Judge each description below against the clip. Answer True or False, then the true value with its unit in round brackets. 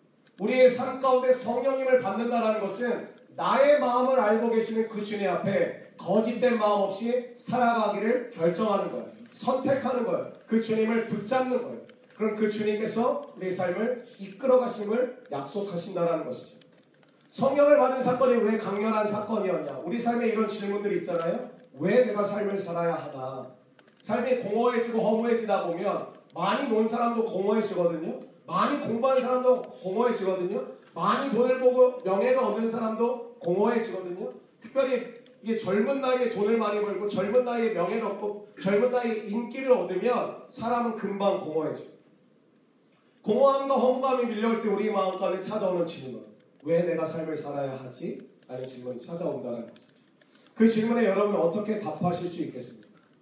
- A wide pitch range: False (4.2 semitones)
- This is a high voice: True (220 Hz)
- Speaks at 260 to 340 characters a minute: False (350 characters per minute)